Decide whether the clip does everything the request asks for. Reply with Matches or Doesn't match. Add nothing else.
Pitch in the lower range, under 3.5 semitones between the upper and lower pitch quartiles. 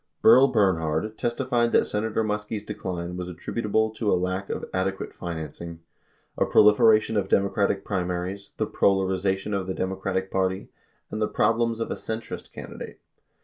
Matches